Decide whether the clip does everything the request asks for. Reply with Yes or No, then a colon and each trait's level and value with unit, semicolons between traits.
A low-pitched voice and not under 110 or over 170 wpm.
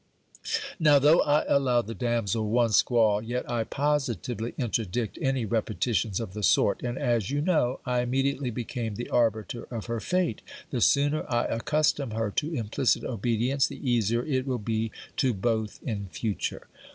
Yes: low, 120 Hz; average, 165 wpm